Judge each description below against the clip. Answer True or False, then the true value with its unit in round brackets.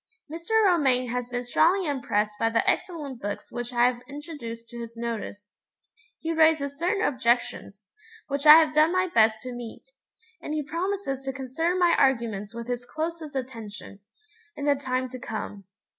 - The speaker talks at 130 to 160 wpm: False (170 wpm)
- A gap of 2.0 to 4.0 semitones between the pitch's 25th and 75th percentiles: False (5.1 semitones)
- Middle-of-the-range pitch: False (260 Hz)